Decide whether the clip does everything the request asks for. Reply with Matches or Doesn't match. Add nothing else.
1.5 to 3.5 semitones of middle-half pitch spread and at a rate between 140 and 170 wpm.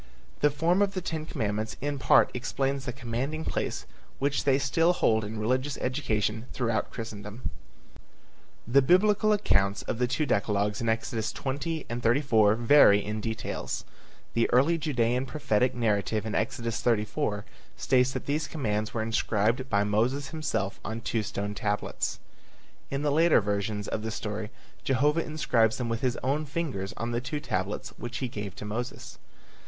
Doesn't match